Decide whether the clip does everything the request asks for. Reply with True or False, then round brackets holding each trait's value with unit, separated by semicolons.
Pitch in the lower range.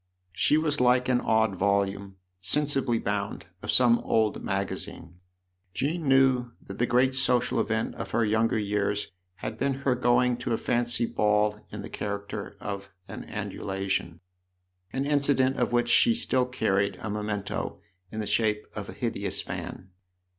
True (115 Hz)